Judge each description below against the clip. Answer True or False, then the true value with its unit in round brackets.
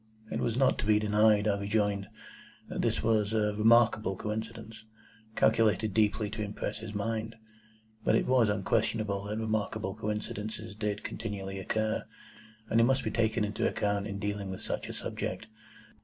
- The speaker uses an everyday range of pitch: False (1.4 semitones)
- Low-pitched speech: True (105 Hz)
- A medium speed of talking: True (160 wpm)